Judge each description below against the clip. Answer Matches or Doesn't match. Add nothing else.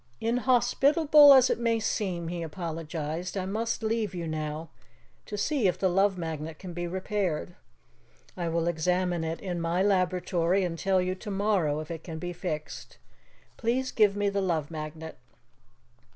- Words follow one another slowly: Doesn't match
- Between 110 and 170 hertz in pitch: Doesn't match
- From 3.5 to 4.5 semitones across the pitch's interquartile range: Matches